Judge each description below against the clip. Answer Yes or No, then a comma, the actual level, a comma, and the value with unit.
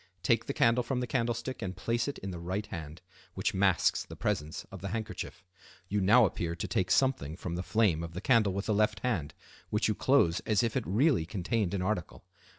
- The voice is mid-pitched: No, low, 100 Hz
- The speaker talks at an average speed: No, fast, 220 wpm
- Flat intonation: No, average, 4.5 semitones